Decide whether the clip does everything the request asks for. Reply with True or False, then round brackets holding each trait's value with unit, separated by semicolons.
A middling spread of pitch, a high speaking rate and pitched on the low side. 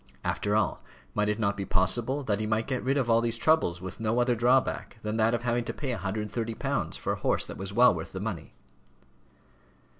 True (3.0 semitones; 215 wpm; 110 Hz)